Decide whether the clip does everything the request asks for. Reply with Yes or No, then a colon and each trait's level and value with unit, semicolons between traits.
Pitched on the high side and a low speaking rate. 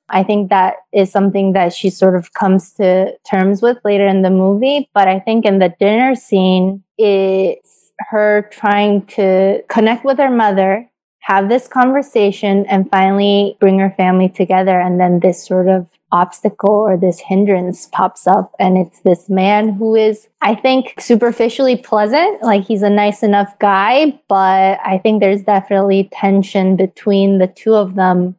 No: high, 195 Hz; average, 165 wpm